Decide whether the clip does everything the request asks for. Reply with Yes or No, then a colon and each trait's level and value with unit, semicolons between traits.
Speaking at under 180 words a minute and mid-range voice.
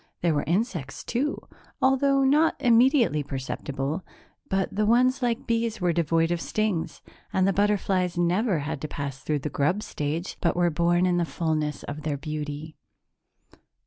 Yes: average, 160 wpm; medium, 175 Hz